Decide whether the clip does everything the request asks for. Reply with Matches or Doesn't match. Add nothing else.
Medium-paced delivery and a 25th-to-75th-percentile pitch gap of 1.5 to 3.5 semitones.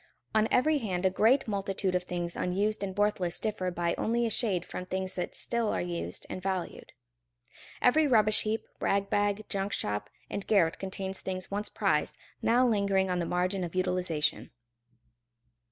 Matches